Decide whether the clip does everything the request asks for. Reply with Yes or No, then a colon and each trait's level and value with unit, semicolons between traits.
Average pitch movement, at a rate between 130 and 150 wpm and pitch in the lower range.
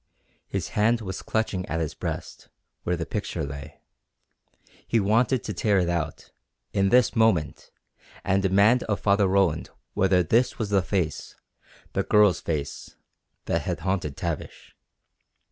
Yes: average, 3.9 semitones; average, 145 wpm; very low, 95 Hz